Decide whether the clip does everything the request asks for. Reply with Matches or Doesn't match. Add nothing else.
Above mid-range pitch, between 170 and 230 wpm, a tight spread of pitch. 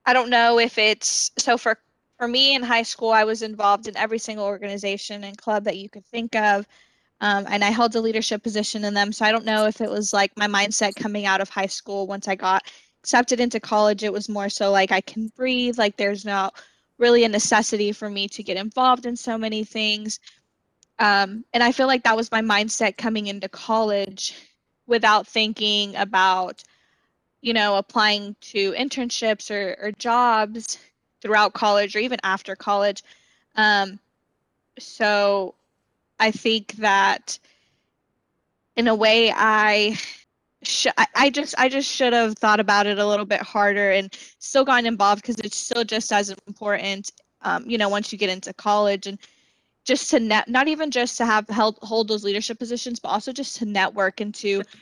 Matches